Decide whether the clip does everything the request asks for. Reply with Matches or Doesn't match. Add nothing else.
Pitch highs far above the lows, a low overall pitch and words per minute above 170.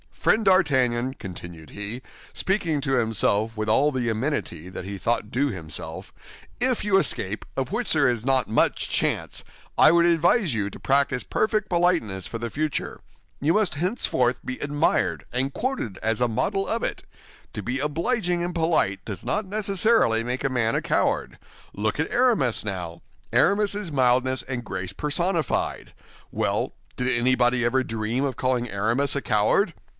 Doesn't match